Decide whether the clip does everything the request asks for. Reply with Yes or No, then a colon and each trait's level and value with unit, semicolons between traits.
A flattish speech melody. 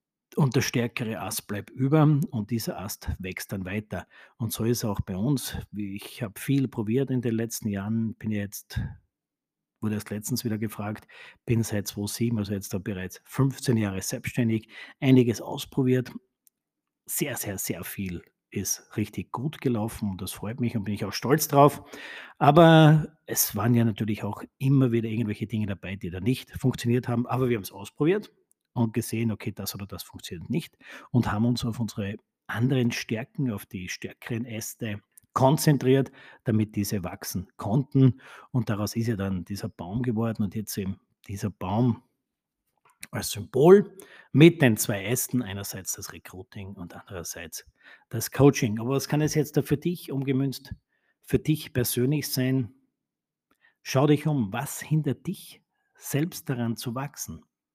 No: average, 4.2 semitones